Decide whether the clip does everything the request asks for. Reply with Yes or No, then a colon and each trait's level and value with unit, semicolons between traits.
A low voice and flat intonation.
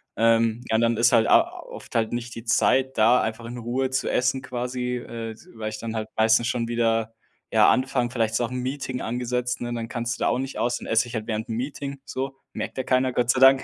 Yes: low, 120 Hz; narrow, 2.0 semitones